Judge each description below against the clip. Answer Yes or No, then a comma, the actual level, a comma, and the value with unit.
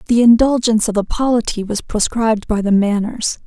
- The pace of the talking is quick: No, average, 175 wpm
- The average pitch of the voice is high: Yes, high, 220 Hz